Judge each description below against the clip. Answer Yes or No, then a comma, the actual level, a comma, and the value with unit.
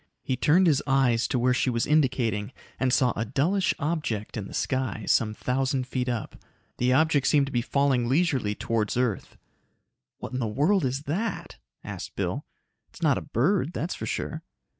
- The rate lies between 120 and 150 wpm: No, average, 180 wpm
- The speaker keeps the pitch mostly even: No, average, 3.8 semitones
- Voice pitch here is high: No, low, 130 Hz